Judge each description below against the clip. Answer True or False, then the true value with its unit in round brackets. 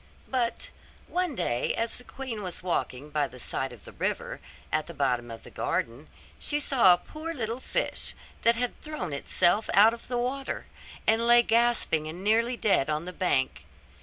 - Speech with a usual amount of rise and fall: False (7.8 semitones)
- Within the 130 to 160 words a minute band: False (185 wpm)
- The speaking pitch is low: False (215 Hz)